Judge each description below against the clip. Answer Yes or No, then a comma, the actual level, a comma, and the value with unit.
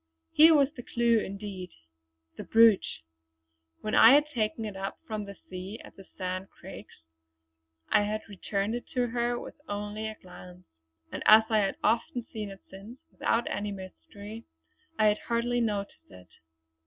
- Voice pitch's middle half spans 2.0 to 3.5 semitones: Yes, average, 2.9 semitones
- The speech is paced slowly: No, average, 165 wpm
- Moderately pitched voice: No, high, 215 Hz